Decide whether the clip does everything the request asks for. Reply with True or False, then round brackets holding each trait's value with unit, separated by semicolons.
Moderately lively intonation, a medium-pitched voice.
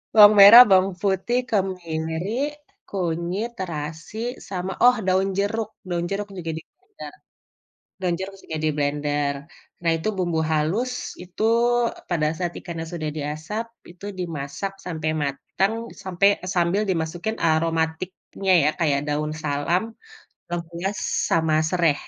True (3.6 semitones; 175 Hz)